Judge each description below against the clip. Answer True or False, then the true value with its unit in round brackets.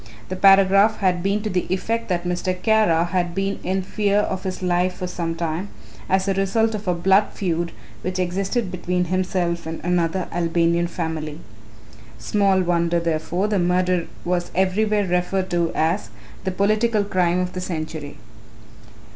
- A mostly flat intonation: True (2.1 semitones)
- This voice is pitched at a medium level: True (180 Hz)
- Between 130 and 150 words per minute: False (160 wpm)